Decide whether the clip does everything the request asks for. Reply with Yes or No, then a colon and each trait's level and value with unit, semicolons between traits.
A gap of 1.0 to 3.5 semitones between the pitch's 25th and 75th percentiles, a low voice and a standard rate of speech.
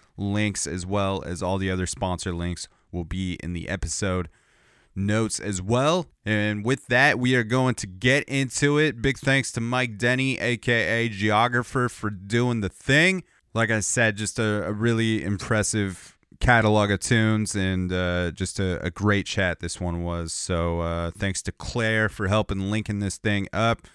No: average, 4.3 semitones; low, 105 Hz; average, 175 wpm